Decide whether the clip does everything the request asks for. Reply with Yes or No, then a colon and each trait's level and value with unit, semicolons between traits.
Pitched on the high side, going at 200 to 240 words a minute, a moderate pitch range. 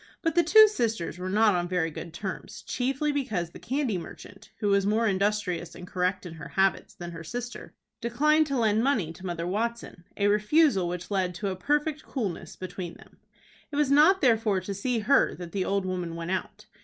No: high, 200 Hz; fast, 205 wpm; wide, 5.7 semitones